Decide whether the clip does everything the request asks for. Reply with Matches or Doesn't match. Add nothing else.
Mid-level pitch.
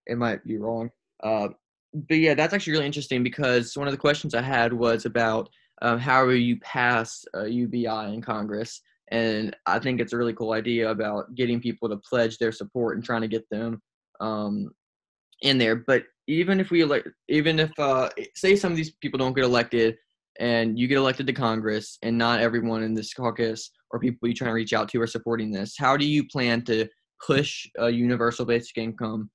Doesn't match